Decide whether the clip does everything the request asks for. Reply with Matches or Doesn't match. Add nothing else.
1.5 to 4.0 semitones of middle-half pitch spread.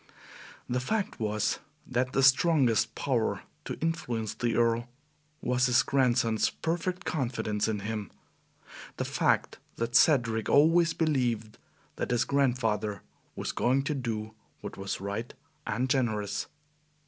Matches